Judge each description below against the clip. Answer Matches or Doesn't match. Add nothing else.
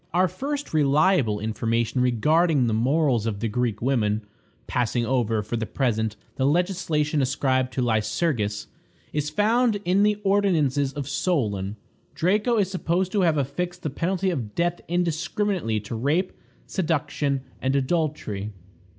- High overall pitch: Doesn't match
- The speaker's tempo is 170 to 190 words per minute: Doesn't match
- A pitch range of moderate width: Doesn't match